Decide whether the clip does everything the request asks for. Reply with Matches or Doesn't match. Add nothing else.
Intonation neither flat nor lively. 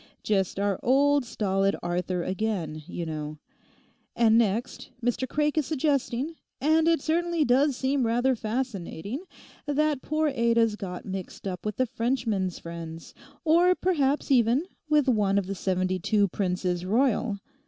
Doesn't match